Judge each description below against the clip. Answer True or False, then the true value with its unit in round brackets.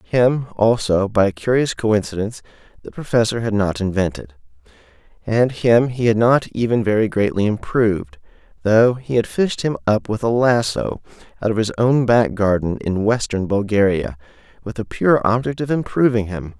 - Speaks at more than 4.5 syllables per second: True (4.9 syllables/s)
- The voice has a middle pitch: False (110 Hz)